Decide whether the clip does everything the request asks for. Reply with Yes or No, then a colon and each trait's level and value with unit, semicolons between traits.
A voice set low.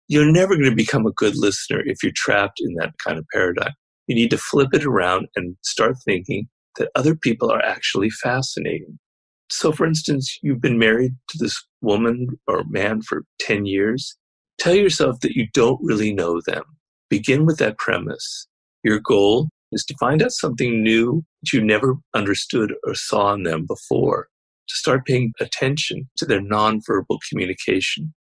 Yes: low, 125 Hz